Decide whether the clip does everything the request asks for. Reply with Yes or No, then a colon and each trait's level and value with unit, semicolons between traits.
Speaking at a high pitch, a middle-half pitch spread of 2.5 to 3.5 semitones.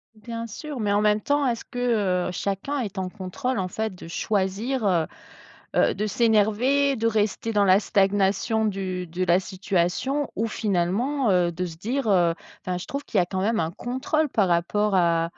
No: high, 205 Hz; average, 4.1 semitones